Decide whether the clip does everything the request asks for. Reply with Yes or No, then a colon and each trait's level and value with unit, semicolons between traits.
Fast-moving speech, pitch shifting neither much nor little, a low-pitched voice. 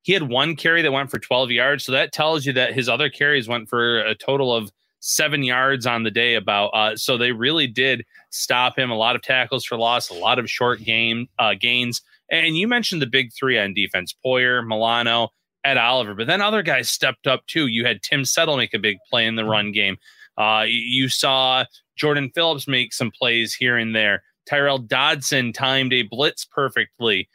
Yes: fast, 210 wpm; average, 3.1 semitones; low, 125 Hz